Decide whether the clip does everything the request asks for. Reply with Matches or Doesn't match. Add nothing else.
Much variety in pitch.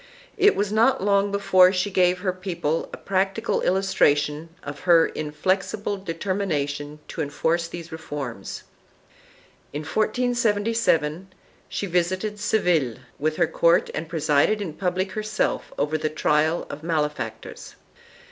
Doesn't match